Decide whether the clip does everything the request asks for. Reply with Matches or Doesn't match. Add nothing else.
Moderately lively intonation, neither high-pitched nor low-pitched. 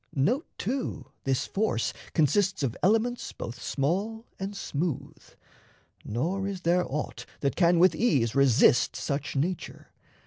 Doesn't match